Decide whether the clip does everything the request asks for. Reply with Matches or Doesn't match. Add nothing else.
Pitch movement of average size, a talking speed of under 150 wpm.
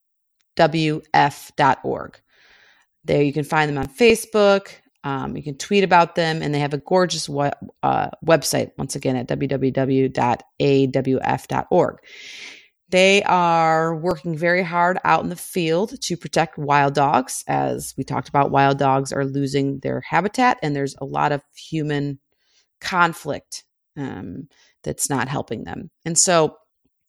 Matches